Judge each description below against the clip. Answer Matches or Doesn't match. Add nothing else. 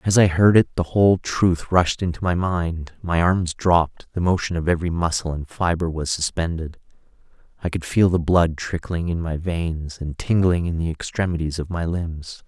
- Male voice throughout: Matches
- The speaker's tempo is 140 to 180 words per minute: Doesn't match